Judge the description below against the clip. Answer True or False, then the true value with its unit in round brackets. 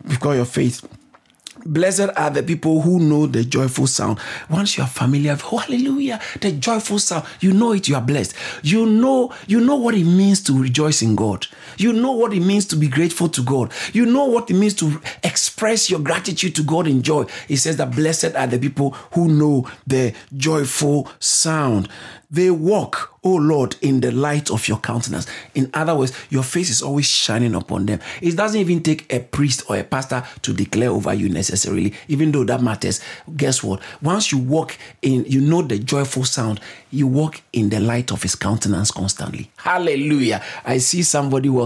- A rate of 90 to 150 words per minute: False (195 wpm)